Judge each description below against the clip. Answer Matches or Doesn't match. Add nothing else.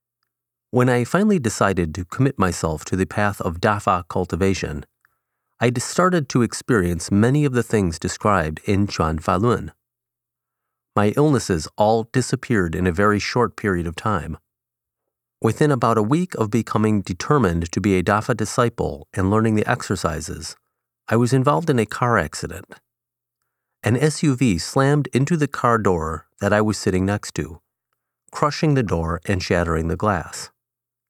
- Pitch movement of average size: Matches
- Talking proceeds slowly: Doesn't match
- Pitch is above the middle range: Doesn't match